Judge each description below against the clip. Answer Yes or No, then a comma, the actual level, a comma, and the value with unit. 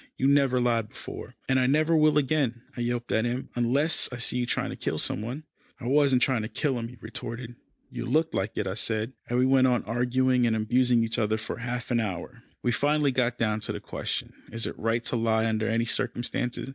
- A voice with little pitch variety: Yes, narrow, 2.3 semitones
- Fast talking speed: Yes, fast, 230 wpm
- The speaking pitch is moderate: No, low, 120 Hz